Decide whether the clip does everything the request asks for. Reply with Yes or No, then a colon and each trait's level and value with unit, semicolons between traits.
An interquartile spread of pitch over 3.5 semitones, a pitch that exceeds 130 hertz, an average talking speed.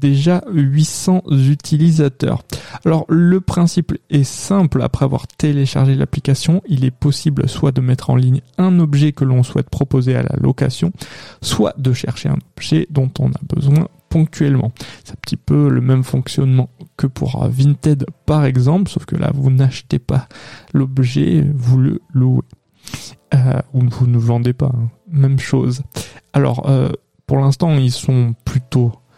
No: average, 2.9 semitones; medium, 140 Hz; average, 160 wpm